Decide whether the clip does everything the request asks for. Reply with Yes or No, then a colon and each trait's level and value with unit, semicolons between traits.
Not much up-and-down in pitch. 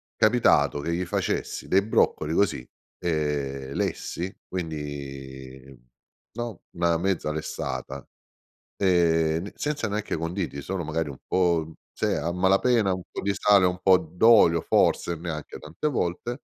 No: average, 4.2 semitones